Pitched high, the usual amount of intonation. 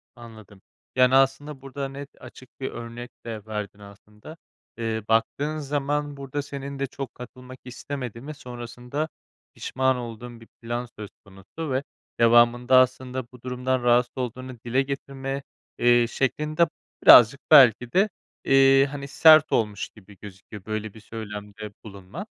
No: low, 125 Hz; average, 3.3 semitones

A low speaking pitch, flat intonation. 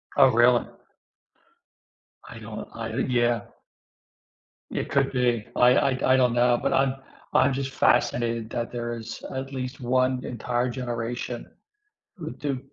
Yes: low, 125 Hz; narrow, 1.6 semitones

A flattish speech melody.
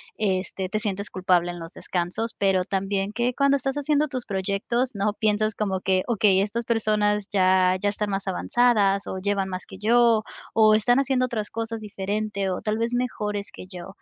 No: average, 3.0 semitones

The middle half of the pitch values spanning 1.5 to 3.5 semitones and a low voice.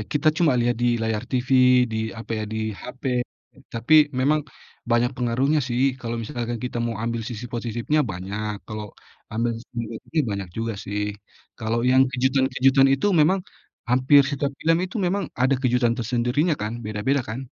Yes: average, 3.0 semitones; low, 120 Hz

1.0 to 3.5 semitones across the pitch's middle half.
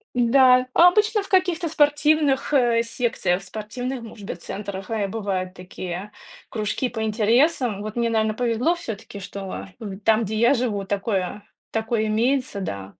No: average, 4.2 semitones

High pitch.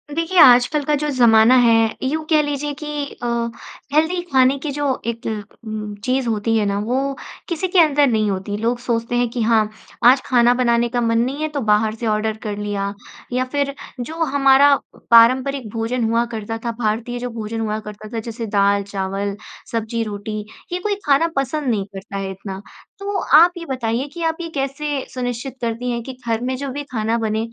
Yes: high, 240 Hz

